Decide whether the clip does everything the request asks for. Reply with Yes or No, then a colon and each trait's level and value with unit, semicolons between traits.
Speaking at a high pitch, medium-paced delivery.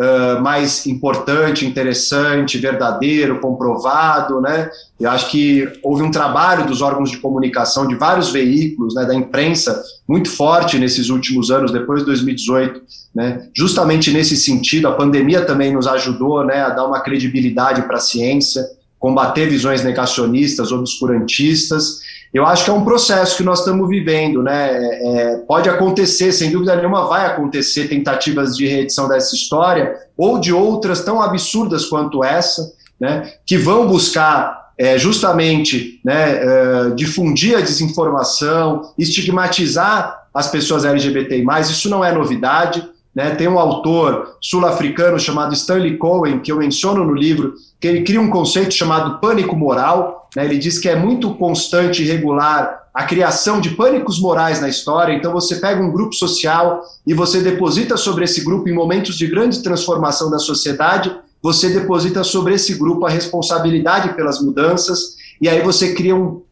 No: medium, 155 Hz; average, 155 wpm